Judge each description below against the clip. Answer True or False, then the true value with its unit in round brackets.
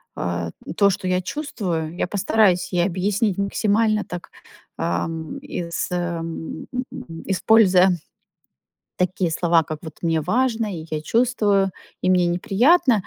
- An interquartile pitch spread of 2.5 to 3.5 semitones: False (4.0 semitones)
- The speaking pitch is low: False (185 Hz)